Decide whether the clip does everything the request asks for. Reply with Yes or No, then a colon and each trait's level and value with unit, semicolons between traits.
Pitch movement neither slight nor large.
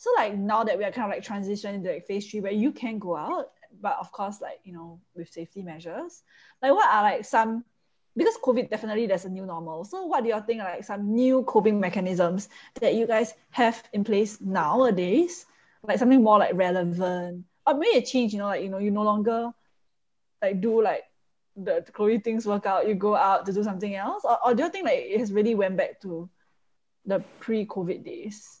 Yes: average, 3.3 semitones